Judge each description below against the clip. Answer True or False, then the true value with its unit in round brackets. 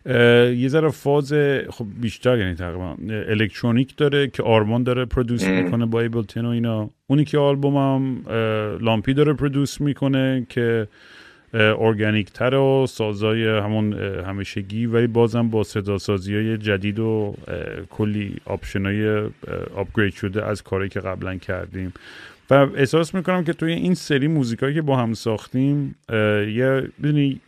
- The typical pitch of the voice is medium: False (115 Hz)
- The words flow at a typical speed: True (140 wpm)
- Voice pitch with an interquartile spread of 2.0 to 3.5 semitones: False (4.3 semitones)